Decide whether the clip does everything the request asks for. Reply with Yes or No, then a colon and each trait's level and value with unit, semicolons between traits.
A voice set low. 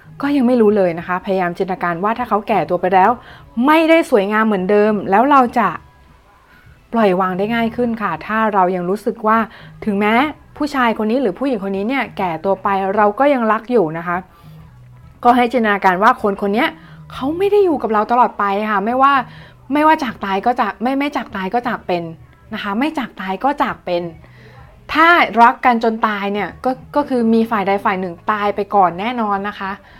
No: high, 215 Hz